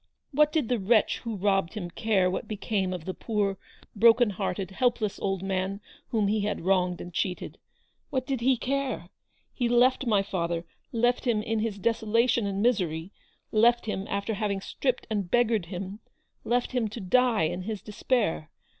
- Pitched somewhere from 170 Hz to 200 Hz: No, high, 210 Hz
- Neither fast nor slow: Yes, average, 170 wpm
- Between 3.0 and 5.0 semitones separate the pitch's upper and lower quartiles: Yes, average, 3.8 semitones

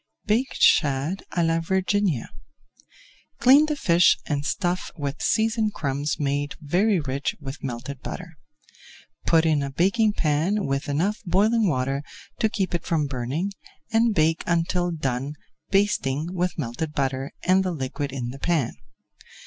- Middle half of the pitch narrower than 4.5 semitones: No, average, 5.3 semitones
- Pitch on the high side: No, medium, 165 Hz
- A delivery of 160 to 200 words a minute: No, average, 145 wpm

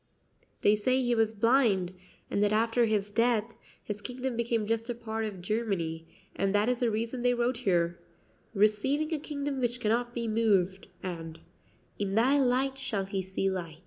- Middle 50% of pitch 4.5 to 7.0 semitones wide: No, average, 3.7 semitones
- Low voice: No, high, 225 Hz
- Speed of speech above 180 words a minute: No, average, 175 wpm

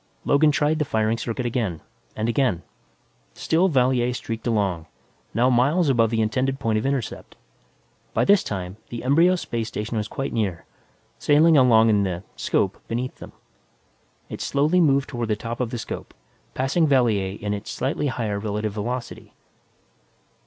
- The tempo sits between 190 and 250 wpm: No, average, 160 wpm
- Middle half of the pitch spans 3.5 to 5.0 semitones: Yes, average, 4.0 semitones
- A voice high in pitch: No, low, 120 Hz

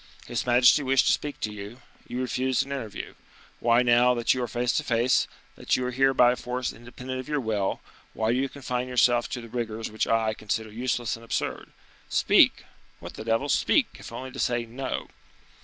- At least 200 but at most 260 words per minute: Yes, fast, 205 wpm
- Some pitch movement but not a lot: No, narrow, 2.0 semitones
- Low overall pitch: Yes, low, 120 Hz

